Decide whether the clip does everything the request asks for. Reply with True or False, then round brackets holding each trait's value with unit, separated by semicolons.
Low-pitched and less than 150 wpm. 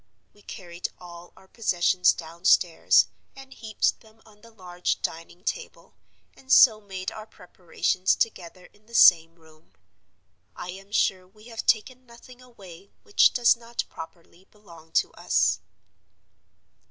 False (190 Hz; 140 wpm)